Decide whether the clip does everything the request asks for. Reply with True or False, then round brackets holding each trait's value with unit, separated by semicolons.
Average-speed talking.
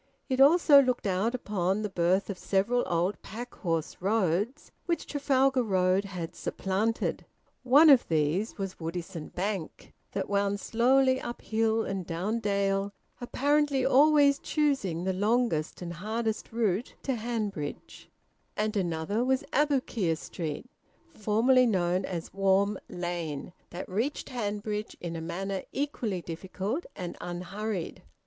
False (130 wpm)